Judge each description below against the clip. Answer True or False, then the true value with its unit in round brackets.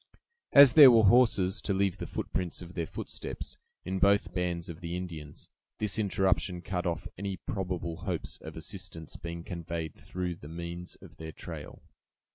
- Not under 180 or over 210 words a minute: False (165 wpm)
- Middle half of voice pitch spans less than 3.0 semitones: True (2.5 semitones)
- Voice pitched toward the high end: False (90 Hz)